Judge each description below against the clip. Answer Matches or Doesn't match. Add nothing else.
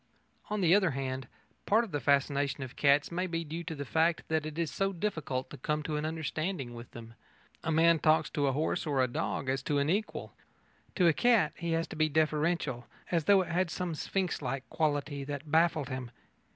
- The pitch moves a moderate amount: Matches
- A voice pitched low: Doesn't match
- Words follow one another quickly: Matches